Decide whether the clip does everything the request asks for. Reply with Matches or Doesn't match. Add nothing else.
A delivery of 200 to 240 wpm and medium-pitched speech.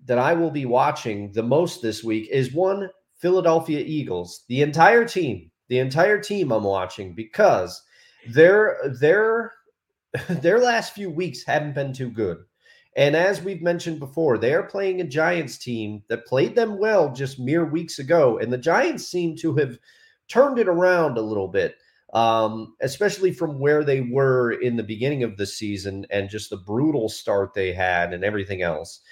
Doesn't match